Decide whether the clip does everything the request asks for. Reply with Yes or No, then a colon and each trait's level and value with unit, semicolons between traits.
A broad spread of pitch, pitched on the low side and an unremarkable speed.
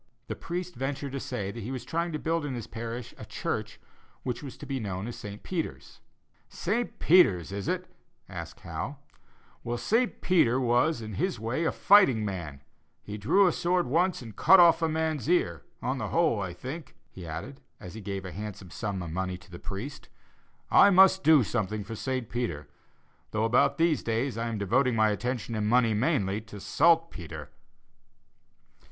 Yes: wide, 7.7 semitones; low, 120 Hz; average, 185 wpm